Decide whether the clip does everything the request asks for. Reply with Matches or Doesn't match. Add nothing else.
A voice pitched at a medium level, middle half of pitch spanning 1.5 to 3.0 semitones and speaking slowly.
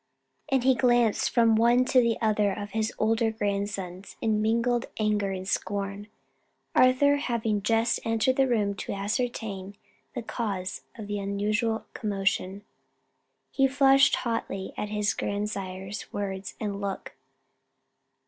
Doesn't match